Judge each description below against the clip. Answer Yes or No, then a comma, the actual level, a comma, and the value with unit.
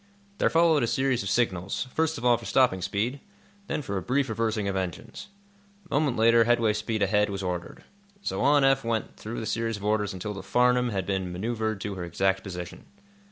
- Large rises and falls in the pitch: No, average, 4.1 semitones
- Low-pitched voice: Yes, low, 110 Hz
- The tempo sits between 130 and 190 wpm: No, fast, 205 wpm